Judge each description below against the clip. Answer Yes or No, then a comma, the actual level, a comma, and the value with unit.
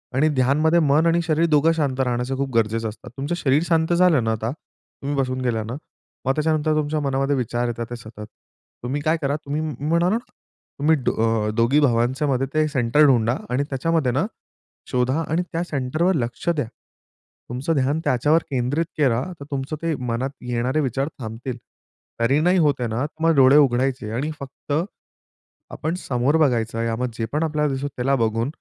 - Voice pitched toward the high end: No, low, 135 Hz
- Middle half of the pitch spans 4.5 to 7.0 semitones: No, average, 4.0 semitones